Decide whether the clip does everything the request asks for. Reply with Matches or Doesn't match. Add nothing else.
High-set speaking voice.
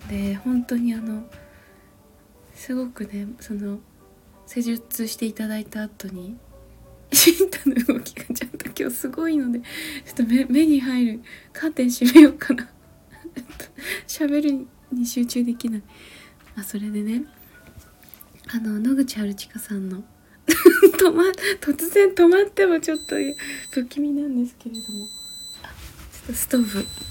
Matches